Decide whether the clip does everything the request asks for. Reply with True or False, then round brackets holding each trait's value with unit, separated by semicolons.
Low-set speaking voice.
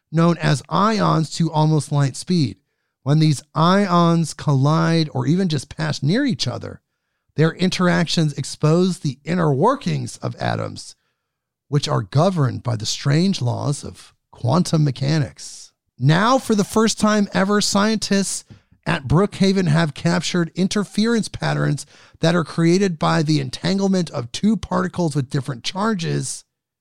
False (160 Hz)